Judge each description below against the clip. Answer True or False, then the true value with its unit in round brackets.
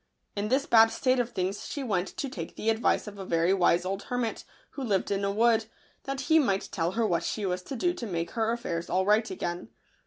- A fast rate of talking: True (240 wpm)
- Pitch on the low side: False (210 Hz)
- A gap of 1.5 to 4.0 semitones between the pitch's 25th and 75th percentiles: False (4.4 semitones)